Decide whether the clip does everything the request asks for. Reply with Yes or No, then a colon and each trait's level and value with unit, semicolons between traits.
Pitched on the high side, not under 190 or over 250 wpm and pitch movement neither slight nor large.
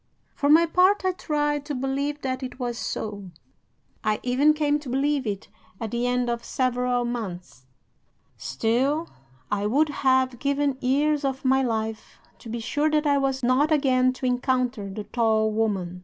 No: very high, 255 Hz; average, 170 wpm; average, 3.9 semitones